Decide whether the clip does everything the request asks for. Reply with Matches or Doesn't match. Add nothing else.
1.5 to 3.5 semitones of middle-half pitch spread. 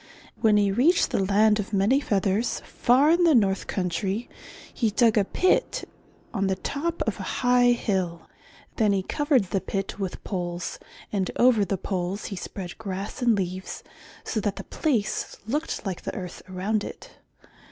Doesn't match